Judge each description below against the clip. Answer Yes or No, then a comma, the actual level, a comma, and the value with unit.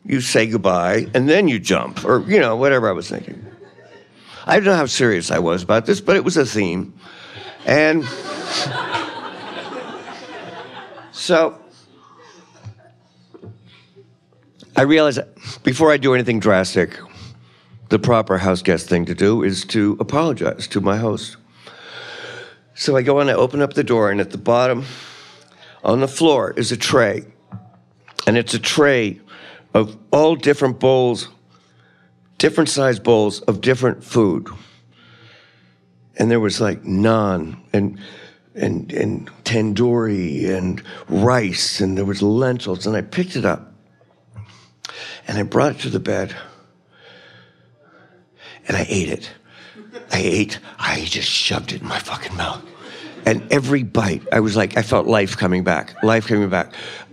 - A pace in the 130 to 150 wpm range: Yes, average, 145 wpm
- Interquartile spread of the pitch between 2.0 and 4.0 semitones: No, wide, 5.5 semitones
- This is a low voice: Yes, low, 110 Hz